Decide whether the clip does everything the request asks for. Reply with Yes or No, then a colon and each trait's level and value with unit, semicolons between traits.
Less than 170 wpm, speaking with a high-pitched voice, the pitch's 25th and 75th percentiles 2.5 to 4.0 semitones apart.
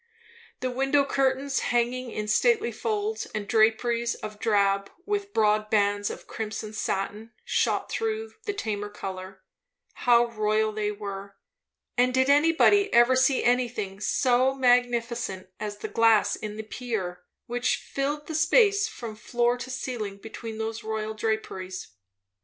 Yes: average, 140 wpm; high, 230 Hz; average, 3.6 semitones